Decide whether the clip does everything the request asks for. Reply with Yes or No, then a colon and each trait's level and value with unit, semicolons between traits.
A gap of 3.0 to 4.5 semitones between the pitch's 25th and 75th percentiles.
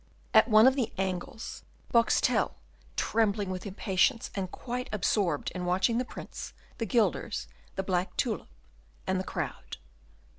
Yes: average, 3.7 semitones